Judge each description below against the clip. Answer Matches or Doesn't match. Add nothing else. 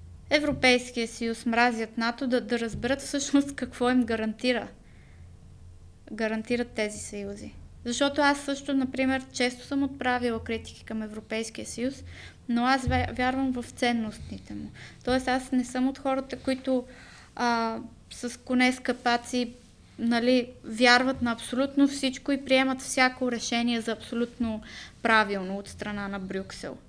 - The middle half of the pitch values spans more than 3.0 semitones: Doesn't match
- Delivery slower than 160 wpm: Matches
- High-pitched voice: Matches